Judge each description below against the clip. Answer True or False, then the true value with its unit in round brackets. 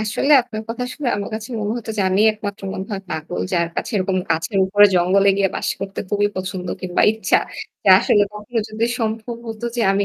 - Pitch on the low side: False (205 Hz)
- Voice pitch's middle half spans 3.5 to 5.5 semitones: False (2.5 semitones)